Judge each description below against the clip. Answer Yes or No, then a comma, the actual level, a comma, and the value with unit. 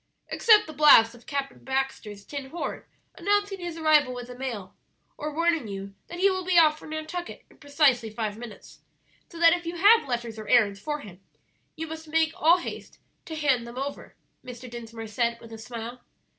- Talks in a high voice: Yes, very high, 275 Hz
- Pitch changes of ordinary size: No, wide, 5.7 semitones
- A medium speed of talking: Yes, average, 195 wpm